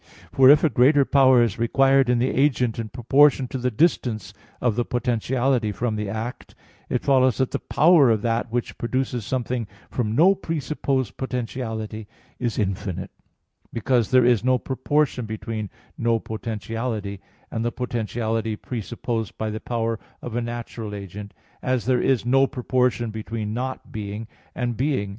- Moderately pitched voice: No, low, 120 Hz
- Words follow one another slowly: No, average, 155 wpm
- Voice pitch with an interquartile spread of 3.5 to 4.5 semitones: No, average, 2.9 semitones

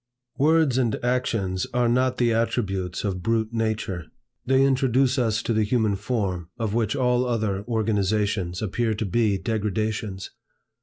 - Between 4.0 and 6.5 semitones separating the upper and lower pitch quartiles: No, average, 3.5 semitones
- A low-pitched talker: Yes, low, 110 Hz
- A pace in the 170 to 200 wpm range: No, average, 145 wpm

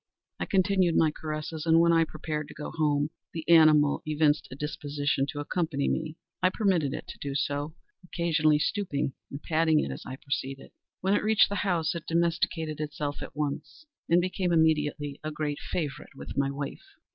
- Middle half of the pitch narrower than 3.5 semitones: Yes, narrow, 2.5 semitones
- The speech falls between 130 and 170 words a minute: No, average, 180 wpm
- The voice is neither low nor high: Yes, medium, 155 Hz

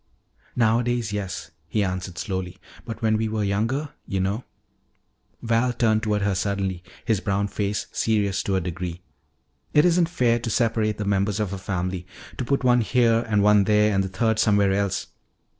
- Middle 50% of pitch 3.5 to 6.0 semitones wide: No, average, 2.9 semitones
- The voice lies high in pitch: No, low, 105 Hz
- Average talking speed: Yes, average, 175 wpm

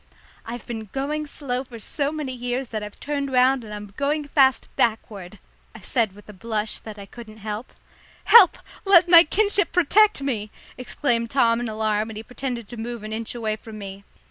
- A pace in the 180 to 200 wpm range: Yes, average, 195 wpm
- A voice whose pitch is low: No, high, 235 Hz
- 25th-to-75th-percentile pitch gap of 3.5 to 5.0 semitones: Yes, average, 4.4 semitones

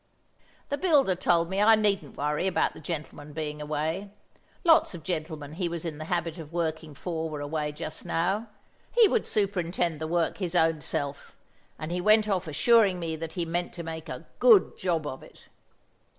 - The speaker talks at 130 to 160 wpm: No, average, 190 wpm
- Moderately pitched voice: Yes, medium, 170 Hz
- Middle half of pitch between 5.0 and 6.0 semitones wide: No, average, 3.5 semitones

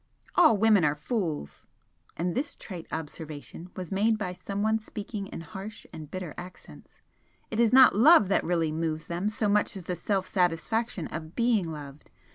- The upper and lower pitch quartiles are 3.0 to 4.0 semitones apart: No, average, 4.8 semitones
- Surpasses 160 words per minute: Yes, average, 170 wpm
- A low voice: No, medium, 185 Hz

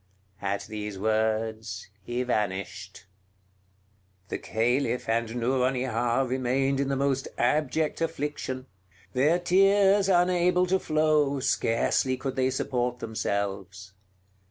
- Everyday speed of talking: No, slow, 105 wpm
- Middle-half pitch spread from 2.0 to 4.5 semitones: No, average, 4.9 semitones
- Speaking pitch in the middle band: No, low, 130 Hz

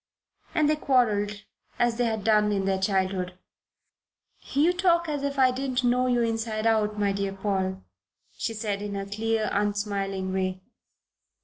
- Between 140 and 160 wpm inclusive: Yes, average, 155 wpm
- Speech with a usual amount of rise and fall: Yes, average, 3.8 semitones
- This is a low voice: No, high, 210 Hz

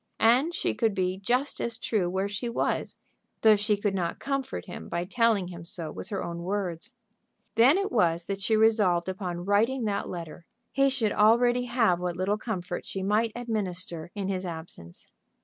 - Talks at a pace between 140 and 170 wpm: No, average, 185 wpm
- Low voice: No, high, 200 Hz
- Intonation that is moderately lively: Yes, average, 4.4 semitones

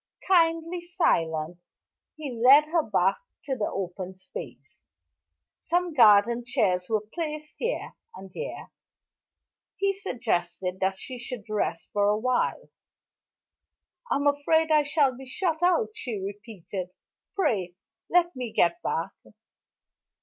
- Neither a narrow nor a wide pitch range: No, wide, 8.8 semitones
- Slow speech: Yes, slow, 120 wpm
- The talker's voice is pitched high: Yes, high, 245 Hz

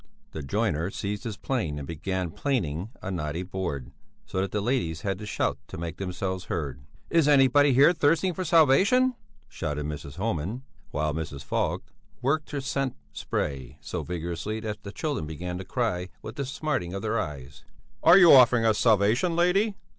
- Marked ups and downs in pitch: Yes, wide, 8.8 semitones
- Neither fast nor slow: Yes, average, 175 wpm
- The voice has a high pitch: No, low, 100 Hz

